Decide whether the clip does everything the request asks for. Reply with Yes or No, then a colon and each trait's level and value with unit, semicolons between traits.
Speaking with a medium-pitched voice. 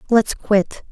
No: high, 210 Hz